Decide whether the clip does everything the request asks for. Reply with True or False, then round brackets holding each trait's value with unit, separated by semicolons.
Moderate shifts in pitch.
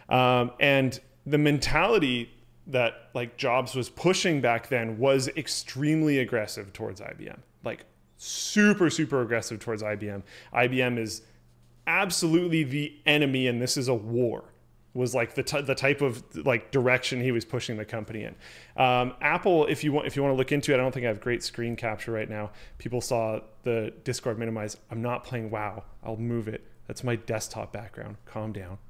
True (3.6 semitones)